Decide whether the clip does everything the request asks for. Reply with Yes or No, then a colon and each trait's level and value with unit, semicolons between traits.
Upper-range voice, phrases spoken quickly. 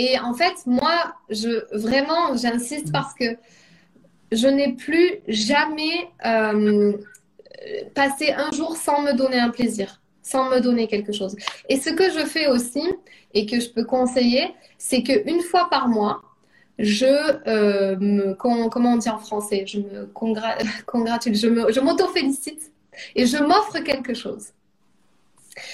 No: very high, 250 Hz; average, 150 wpm